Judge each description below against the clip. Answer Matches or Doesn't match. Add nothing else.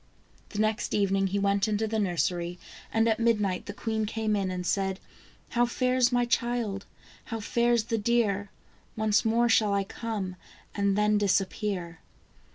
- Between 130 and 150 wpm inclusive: Doesn't match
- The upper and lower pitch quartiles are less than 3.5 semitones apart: Matches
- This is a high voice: Matches